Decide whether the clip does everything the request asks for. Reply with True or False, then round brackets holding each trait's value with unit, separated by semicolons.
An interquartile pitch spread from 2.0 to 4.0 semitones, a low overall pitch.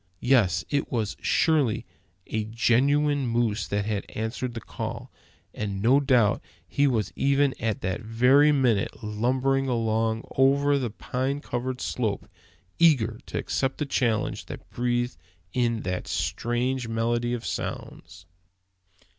True (3.3 semitones; 120 Hz)